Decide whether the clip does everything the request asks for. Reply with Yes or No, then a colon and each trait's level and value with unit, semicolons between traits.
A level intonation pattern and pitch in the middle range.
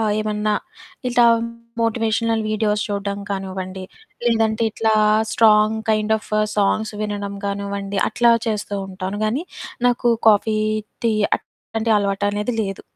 No: narrow, 1.8 semitones; high, 215 Hz